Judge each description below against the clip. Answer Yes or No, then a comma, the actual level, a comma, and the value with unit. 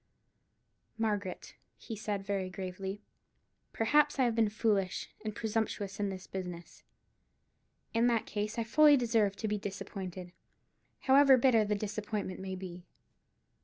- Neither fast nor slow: No, slow, 130 wpm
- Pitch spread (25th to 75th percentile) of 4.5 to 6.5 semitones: No, average, 2.9 semitones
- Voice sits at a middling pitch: No, high, 210 Hz